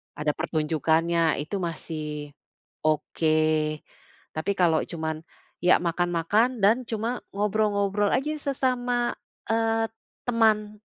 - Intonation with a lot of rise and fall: Yes, wide, 6.0 semitones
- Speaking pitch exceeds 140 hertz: Yes, high, 190 Hz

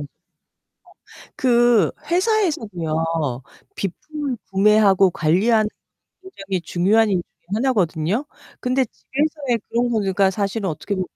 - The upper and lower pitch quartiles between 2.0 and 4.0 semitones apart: No, wide, 5.4 semitones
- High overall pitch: Yes, high, 210 Hz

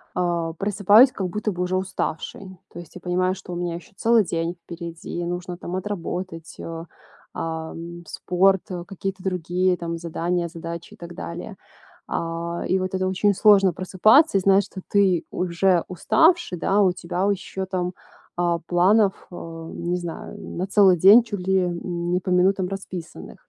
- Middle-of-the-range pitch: Yes, medium, 180 Hz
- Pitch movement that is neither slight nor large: No, narrow, 2.0 semitones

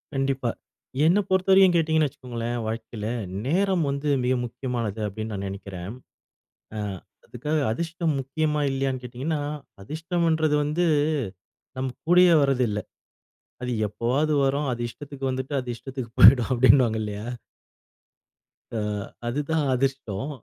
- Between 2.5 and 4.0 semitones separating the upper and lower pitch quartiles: No, average, 4.7 semitones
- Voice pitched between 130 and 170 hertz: Yes, low, 135 Hz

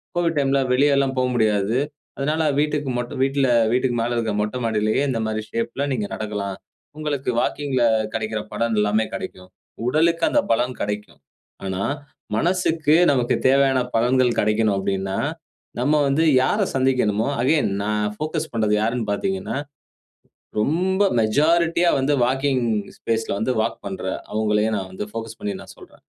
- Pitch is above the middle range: No, low, 120 Hz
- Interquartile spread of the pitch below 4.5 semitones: No, average, 4.9 semitones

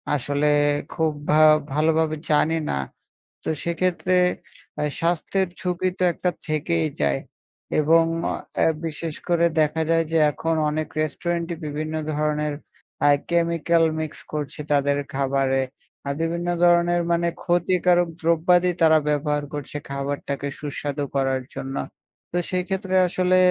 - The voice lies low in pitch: No, medium, 160 Hz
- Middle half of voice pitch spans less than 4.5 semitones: Yes, average, 2.7 semitones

